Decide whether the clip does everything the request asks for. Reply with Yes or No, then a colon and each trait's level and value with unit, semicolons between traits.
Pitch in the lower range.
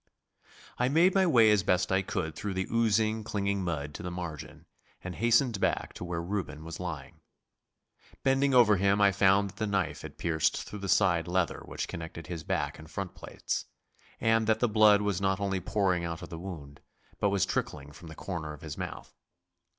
Yes: very low, 95 Hz